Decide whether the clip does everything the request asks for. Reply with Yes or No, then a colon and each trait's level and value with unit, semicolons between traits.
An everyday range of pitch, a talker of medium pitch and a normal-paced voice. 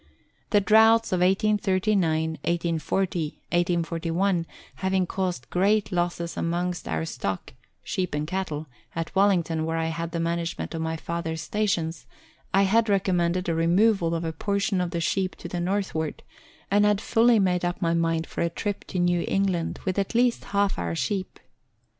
Yes: average, 3.0 semitones; medium, 175 Hz; average, 165 wpm